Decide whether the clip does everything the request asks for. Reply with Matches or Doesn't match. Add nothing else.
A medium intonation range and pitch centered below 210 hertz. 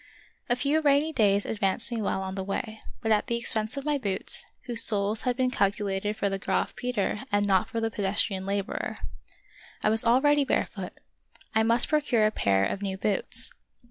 Doesn't match